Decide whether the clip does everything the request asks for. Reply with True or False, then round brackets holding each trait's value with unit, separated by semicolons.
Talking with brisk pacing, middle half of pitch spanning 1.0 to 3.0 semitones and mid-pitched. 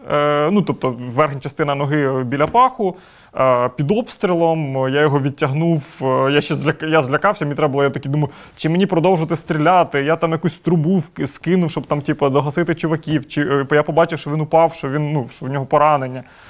True (175 wpm; 2.7 semitones; 150 Hz)